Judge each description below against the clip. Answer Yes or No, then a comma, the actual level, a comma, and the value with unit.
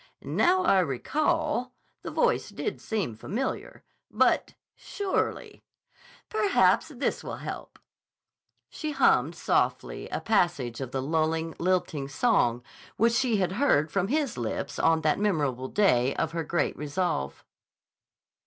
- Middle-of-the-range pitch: Yes, medium, 175 Hz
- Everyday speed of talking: No, slow, 125 wpm